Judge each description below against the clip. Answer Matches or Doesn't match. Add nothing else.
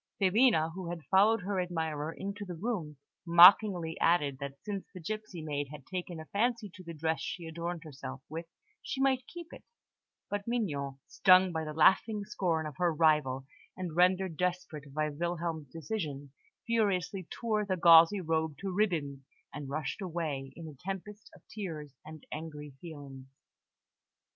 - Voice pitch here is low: Doesn't match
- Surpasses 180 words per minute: Doesn't match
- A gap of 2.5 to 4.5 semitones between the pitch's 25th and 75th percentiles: Matches